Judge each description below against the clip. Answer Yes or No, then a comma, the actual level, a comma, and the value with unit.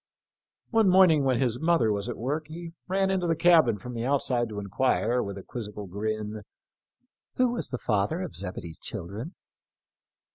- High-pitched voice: No, low, 125 Hz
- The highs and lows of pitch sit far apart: Yes, wide, 8.1 semitones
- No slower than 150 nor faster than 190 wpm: Yes, average, 175 wpm